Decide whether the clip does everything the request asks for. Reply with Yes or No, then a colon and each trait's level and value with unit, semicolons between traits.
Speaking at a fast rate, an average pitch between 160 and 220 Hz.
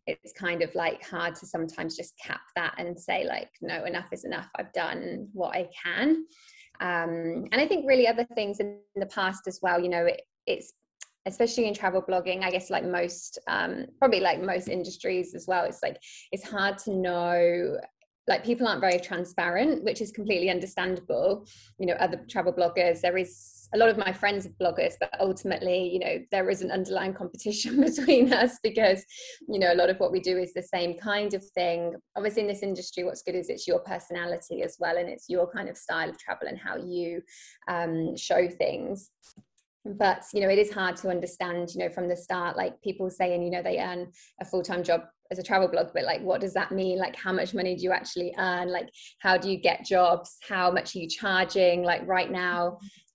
Yes: fast, 215 wpm; medium, 185 Hz